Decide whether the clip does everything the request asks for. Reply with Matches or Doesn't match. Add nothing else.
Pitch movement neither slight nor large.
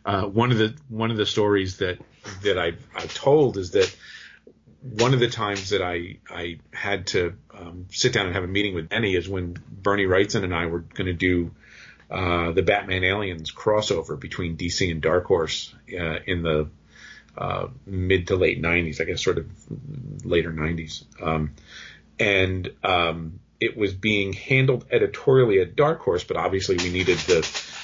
Matches